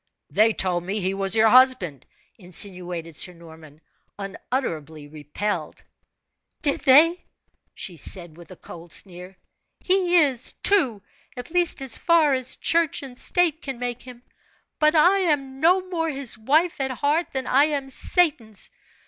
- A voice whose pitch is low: No, very high, 250 Hz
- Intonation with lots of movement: Yes, wide, 8.8 semitones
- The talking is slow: No, average, 150 wpm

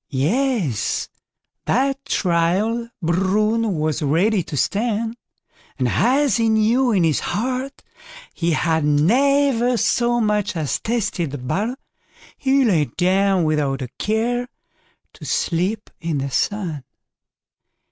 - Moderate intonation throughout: No, wide, 6.6 semitones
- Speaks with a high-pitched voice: Yes, high, 205 Hz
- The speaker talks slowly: Yes, slow, 115 wpm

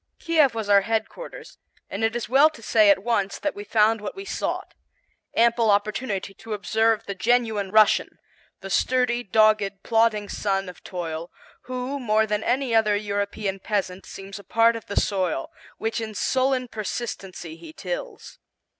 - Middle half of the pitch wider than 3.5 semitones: No, average, 2.9 semitones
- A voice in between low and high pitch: No, high, 215 Hz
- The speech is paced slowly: No, average, 165 wpm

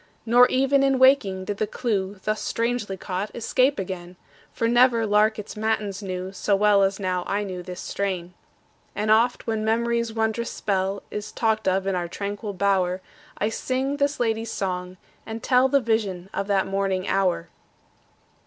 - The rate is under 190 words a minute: Yes, average, 170 wpm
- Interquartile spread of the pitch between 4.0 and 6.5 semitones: No, average, 3.3 semitones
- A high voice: Yes, high, 210 Hz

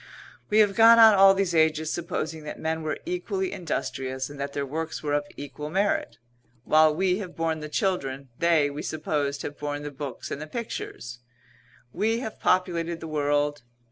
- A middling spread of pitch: Yes, average, 4.0 semitones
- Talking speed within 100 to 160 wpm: No, average, 180 wpm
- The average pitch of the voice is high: No, medium, 155 Hz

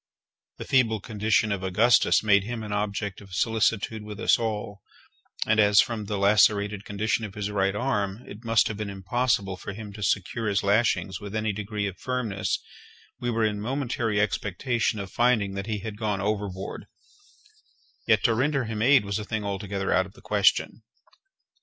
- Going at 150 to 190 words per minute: Yes, average, 180 wpm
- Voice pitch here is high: No, low, 105 Hz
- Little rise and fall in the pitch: Yes, narrow, 2.0 semitones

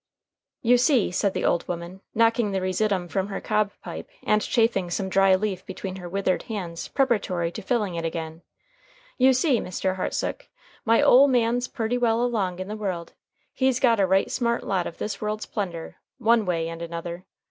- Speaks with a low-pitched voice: No, high, 200 Hz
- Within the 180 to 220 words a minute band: Yes, average, 185 wpm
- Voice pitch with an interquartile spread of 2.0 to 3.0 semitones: No, average, 4.3 semitones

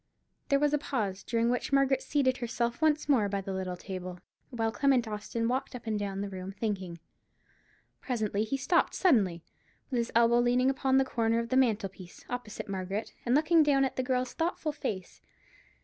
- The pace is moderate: Yes, average, 190 wpm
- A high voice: Yes, high, 235 Hz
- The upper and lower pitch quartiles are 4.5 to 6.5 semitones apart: Yes, average, 4.8 semitones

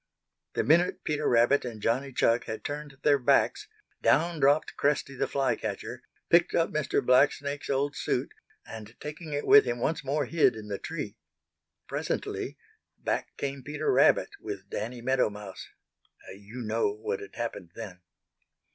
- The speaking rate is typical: Yes, average, 155 wpm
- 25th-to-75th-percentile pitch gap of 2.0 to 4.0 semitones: No, average, 4.6 semitones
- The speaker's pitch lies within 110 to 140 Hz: Yes, low, 135 Hz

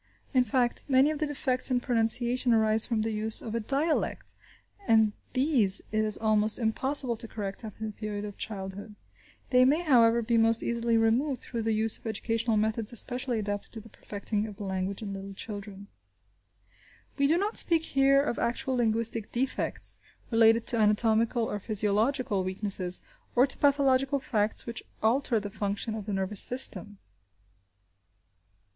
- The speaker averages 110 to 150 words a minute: No, average, 165 wpm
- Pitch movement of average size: Yes, average, 3.2 semitones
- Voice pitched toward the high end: Yes, high, 225 Hz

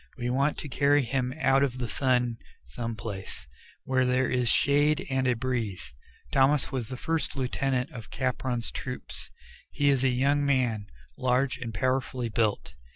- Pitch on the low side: Yes, low, 130 Hz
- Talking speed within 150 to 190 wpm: Yes, average, 160 wpm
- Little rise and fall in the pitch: Yes, narrow, 2.0 semitones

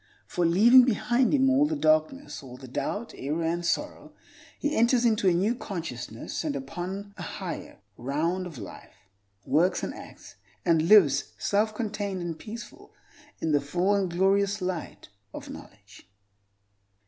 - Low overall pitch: No, medium, 185 Hz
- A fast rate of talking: No, average, 150 wpm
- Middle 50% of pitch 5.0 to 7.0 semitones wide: Yes, wide, 5.4 semitones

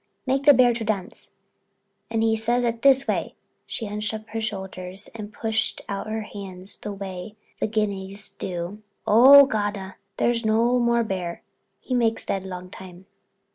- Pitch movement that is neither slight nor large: Yes, average, 3.0 semitones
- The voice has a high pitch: Yes, high, 215 Hz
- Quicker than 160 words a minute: No, average, 155 wpm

